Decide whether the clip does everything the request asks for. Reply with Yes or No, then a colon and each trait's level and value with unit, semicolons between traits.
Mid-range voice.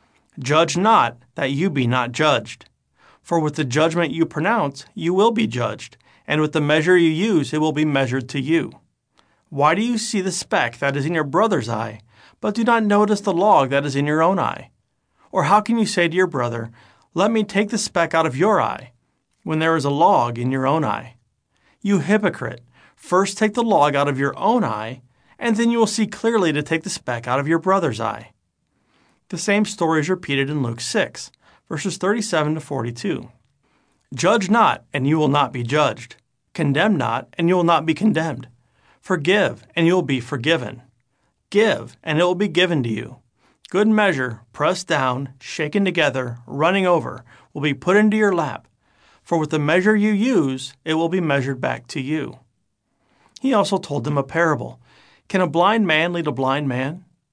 Yes: medium, 155 Hz